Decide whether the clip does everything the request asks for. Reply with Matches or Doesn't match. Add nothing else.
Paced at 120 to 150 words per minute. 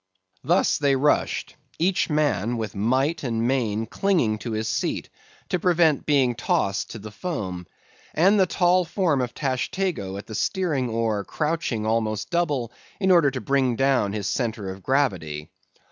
Doesn't match